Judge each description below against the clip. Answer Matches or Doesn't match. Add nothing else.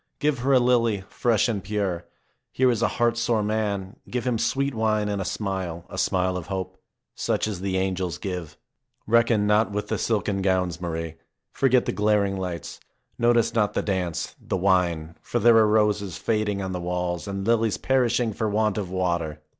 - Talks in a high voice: Doesn't match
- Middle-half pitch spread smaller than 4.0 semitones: Matches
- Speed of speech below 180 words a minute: Doesn't match